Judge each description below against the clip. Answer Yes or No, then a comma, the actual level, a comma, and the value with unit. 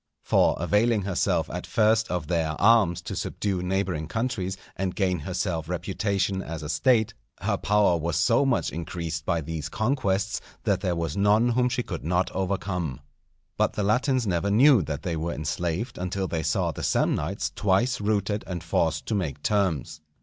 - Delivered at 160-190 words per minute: Yes, average, 170 wpm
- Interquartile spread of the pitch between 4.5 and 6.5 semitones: No, average, 4.0 semitones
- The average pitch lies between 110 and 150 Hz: No, very low, 95 Hz